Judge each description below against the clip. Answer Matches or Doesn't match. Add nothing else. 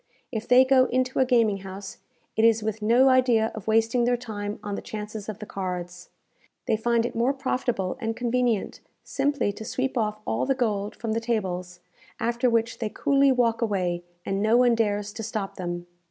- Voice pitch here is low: Doesn't match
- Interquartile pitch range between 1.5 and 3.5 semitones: Matches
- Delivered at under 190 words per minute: Doesn't match